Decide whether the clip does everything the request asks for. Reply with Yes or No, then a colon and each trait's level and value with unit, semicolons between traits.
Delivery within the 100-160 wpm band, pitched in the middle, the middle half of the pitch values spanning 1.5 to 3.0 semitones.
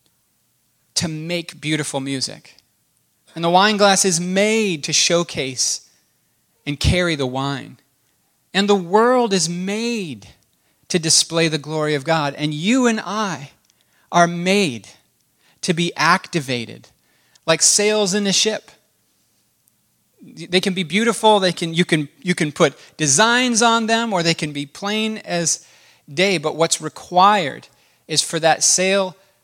No: average, 140 wpm; medium, 175 Hz; average, 4.6 semitones